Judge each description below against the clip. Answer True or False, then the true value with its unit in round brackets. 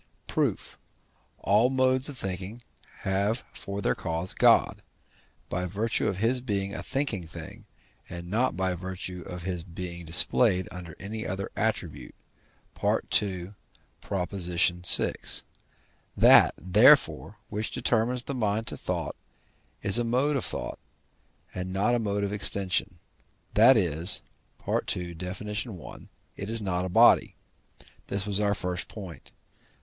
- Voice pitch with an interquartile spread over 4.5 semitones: False (3.5 semitones)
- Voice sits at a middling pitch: False (100 Hz)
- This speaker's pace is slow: True (130 wpm)